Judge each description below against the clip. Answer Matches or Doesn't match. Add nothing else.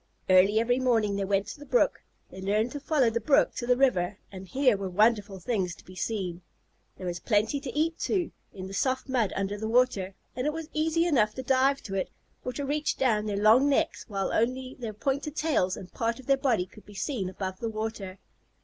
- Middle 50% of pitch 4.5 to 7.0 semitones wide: Matches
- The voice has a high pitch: Matches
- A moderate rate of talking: Doesn't match